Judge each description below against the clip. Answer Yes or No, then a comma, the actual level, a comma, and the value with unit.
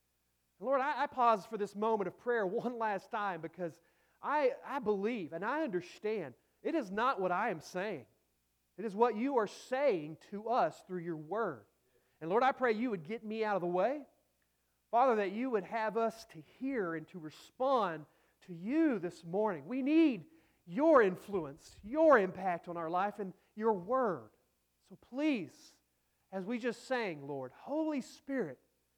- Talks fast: No, average, 175 wpm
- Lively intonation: Yes, wide, 6.6 semitones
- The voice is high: Yes, high, 210 Hz